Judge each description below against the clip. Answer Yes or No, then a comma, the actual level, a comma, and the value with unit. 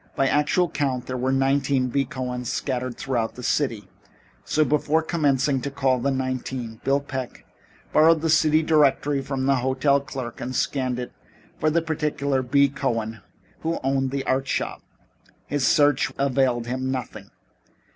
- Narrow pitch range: Yes, narrow, 2.1 semitones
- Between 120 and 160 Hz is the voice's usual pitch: Yes, low, 135 Hz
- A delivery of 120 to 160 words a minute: Yes, average, 155 wpm